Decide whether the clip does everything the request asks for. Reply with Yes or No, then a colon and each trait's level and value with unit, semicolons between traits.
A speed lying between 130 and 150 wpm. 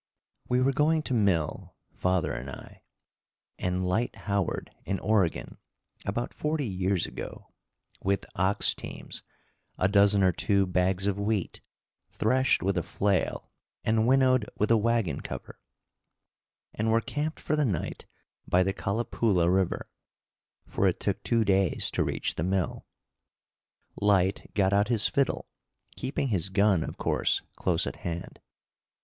Yes: average, 145 wpm